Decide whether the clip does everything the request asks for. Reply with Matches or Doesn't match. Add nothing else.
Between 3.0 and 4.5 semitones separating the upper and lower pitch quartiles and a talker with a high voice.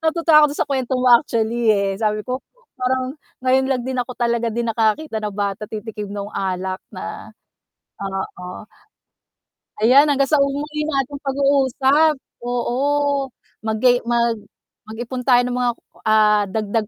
Matches